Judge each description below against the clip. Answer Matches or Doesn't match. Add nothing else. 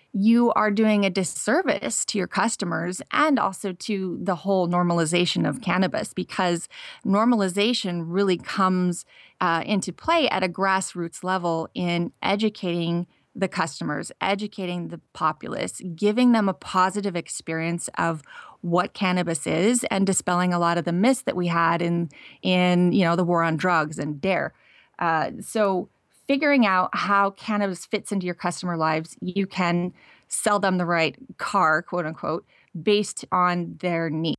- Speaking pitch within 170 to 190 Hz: Matches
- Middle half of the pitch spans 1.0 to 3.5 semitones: Matches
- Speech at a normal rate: Matches